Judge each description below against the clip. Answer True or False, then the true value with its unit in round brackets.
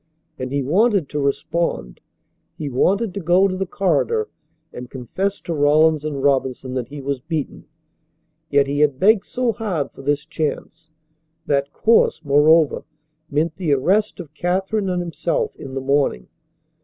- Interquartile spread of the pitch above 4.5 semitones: True (5.2 semitones)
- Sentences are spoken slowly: False (155 wpm)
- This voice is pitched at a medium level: True (155 Hz)